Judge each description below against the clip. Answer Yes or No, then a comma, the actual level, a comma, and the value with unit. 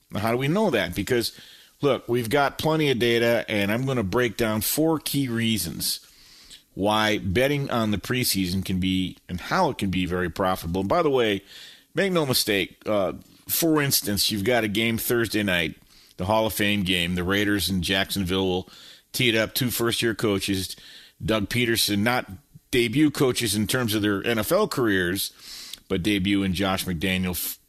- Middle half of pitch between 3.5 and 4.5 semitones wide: Yes, average, 4.0 semitones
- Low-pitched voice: Yes, low, 105 Hz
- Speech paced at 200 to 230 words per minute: No, average, 180 wpm